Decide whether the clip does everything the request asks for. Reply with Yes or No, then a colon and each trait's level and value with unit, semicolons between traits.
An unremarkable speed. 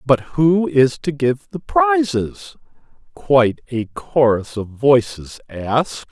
No: slow, 130 wpm